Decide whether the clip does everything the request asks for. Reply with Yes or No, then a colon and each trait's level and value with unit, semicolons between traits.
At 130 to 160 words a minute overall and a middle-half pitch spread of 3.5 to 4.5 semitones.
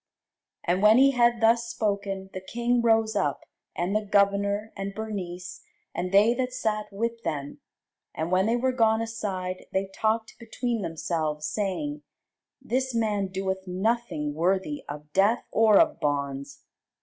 Yes: average, 150 wpm; average, 3.8 semitones